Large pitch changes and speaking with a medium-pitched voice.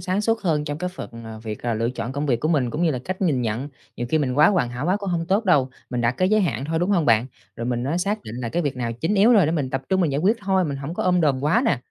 Yes: wide, 6.7 semitones; medium, 150 Hz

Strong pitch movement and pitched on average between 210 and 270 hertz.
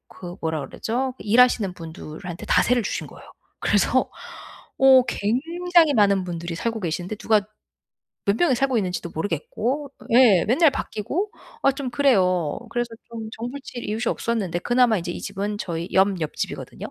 Yes: wide, 5.7 semitones; high, 215 Hz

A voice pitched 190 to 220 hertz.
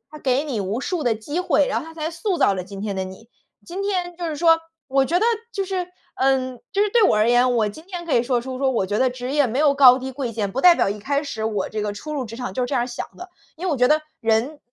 No: very high, 265 Hz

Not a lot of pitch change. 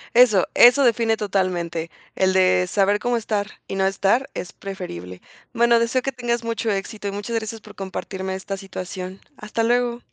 No: average, 3.7 semitones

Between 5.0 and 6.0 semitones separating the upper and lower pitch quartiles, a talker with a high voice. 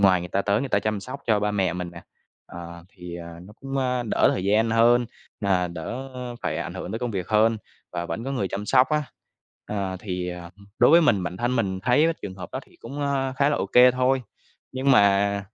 No: wide, 5.4 semitones; low, 105 Hz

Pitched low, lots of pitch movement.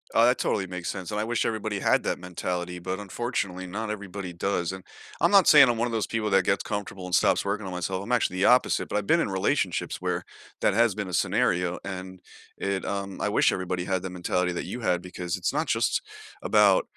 No: very low, 95 Hz; average, 2.9 semitones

